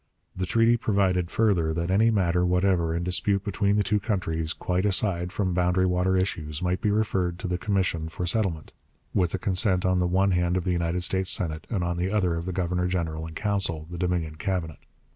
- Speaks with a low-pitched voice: Yes, very low, 90 Hz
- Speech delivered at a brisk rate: Yes, fast, 210 wpm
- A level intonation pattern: Yes, narrow, 2.1 semitones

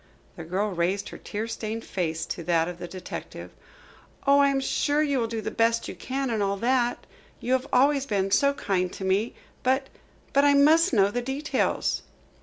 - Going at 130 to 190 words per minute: No, average, 200 wpm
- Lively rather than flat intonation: Yes, wide, 6.0 semitones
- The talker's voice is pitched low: No, high, 230 Hz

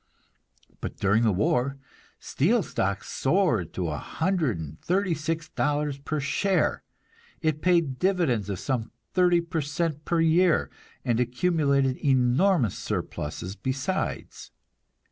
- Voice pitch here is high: No, medium, 145 Hz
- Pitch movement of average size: No, wide, 5.9 semitones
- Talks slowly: Yes, slow, 125 wpm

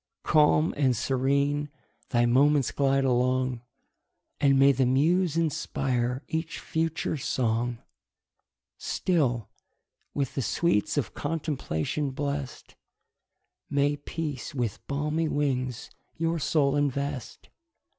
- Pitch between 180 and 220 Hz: No, medium, 140 Hz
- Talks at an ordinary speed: No, slow, 100 wpm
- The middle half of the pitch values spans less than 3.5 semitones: Yes, average, 2.8 semitones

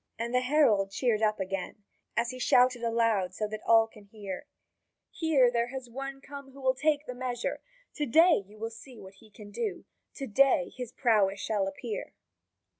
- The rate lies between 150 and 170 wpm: No, average, 190 wpm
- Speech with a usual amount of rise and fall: Yes, average, 4.0 semitones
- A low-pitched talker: No, high, 235 Hz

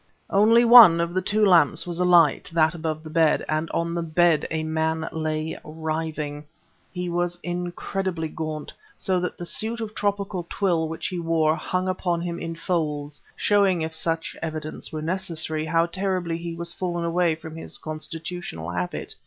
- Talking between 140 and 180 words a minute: Yes, average, 170 wpm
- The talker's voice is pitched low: No, medium, 165 Hz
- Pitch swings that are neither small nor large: No, narrow, 2.1 semitones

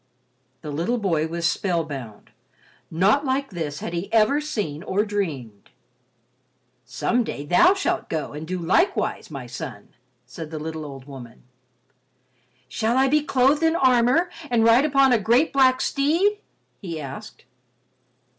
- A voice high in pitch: Yes, high, 200 Hz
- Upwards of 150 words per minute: No, average, 145 wpm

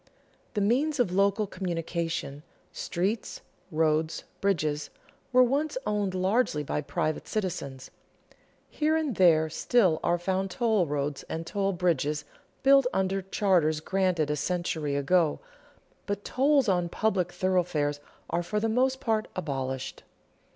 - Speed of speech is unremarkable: No, slow, 130 wpm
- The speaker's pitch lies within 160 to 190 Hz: Yes, medium, 185 Hz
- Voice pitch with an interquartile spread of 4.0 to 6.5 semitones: Yes, average, 5.2 semitones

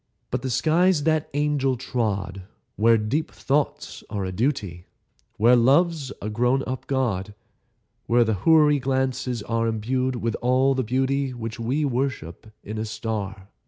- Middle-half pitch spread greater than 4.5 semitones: No, average, 3.8 semitones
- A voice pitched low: Yes, low, 125 Hz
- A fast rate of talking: No, average, 150 wpm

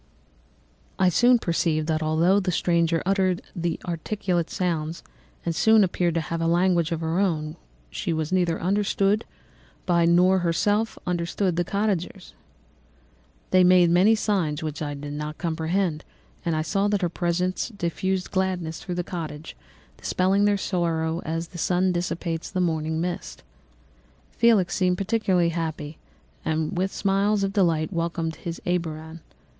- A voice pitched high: No, medium, 175 Hz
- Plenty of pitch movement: No, narrow, 2.6 semitones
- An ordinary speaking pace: Yes, average, 145 wpm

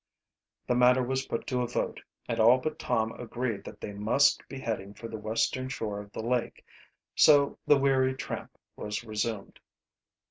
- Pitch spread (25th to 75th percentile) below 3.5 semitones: Yes, average, 3.1 semitones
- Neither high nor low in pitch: No, low, 120 Hz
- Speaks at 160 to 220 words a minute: Yes, average, 175 wpm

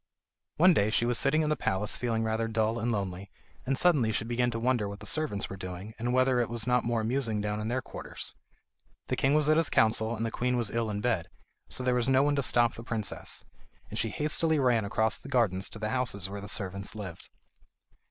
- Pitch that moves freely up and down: No, average, 3.3 semitones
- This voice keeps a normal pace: No, fast, 235 wpm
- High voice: No, low, 115 Hz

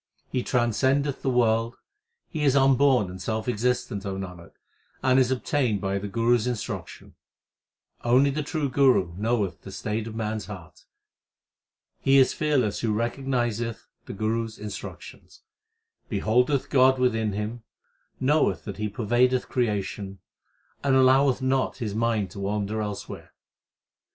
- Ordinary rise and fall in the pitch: Yes, average, 3.8 semitones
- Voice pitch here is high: No, low, 115 Hz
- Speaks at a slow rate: No, average, 145 wpm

